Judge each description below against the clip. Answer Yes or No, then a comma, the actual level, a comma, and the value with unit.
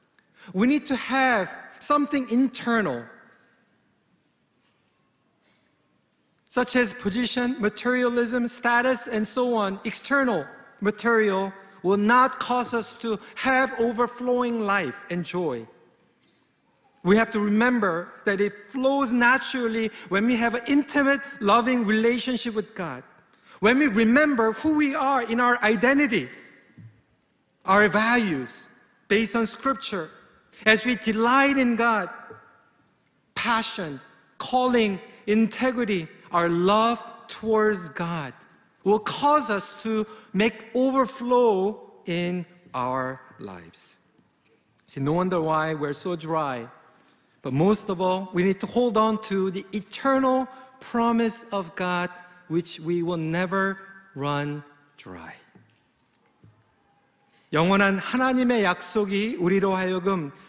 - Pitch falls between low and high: No, high, 220 Hz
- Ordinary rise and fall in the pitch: Yes, average, 4.8 semitones